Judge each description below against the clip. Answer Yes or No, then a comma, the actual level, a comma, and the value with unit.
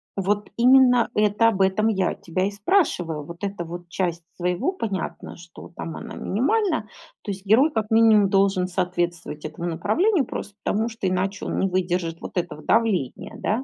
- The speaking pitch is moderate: No, high, 195 Hz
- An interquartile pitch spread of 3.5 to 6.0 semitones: Yes, average, 4.1 semitones